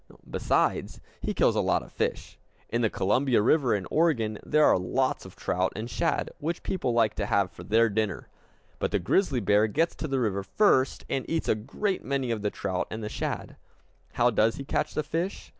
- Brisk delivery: Yes, fast, 210 wpm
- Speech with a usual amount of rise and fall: No, wide, 5.8 semitones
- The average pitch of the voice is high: No, low, 115 Hz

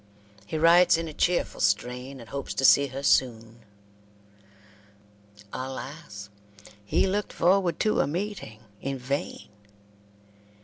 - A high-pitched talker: No, medium, 140 Hz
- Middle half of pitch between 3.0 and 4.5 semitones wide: No, wide, 5.5 semitones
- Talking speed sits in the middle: No, slow, 120 wpm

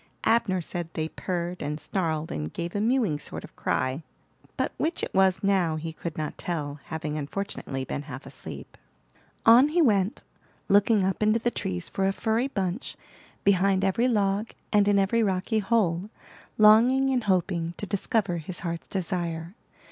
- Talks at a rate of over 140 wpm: Yes, average, 165 wpm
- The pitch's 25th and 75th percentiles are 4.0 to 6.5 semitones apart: Yes, average, 4.4 semitones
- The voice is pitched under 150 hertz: No, high, 190 Hz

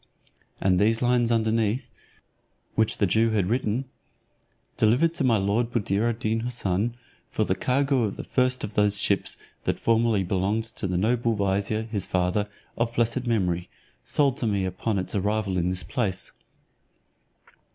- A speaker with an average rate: Yes, average, 160 wpm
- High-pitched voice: No, low, 110 Hz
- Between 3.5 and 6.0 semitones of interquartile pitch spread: No, average, 3.1 semitones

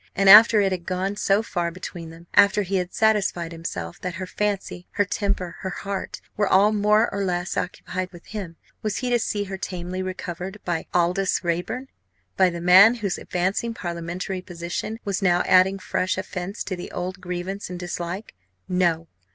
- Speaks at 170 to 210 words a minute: Yes, average, 180 wpm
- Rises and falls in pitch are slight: Yes, narrow, 2.3 semitones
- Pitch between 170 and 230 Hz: Yes, medium, 185 Hz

